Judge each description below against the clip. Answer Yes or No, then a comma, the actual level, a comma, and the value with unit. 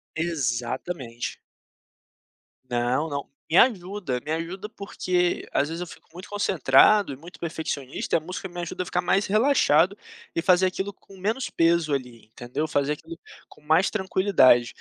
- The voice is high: No, medium, 170 Hz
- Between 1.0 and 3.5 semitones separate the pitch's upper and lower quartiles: No, average, 4.9 semitones